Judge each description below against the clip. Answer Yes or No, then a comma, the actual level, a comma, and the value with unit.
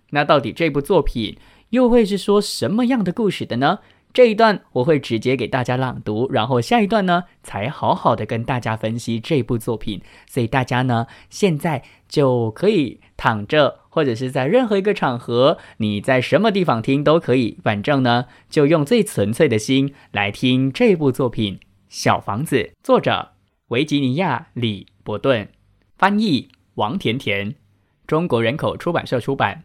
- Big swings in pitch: Yes, wide, 6.6 semitones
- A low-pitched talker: Yes, low, 130 Hz